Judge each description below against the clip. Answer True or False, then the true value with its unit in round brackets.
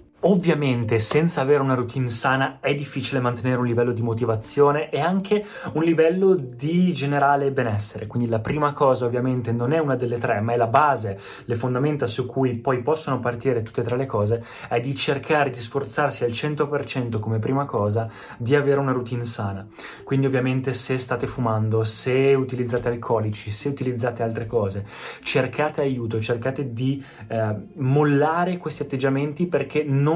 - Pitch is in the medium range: False (130 Hz)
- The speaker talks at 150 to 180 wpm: True (165 wpm)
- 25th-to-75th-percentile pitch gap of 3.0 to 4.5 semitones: True (3.3 semitones)